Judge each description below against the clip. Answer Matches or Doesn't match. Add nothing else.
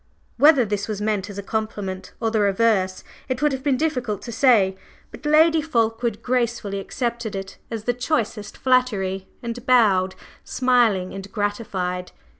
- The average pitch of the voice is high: Matches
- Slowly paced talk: Doesn't match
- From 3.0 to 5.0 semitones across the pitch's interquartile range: Matches